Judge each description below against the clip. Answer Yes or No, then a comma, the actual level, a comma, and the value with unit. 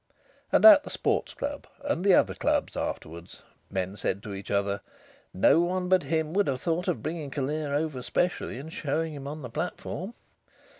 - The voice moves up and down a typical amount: No, wide, 6.0 semitones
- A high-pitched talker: No, medium, 155 Hz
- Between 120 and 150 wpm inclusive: No, average, 185 wpm